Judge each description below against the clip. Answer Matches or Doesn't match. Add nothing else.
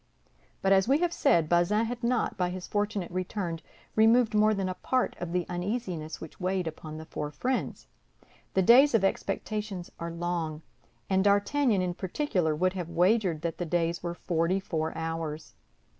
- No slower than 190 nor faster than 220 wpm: Doesn't match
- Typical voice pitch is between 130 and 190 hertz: Matches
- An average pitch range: Matches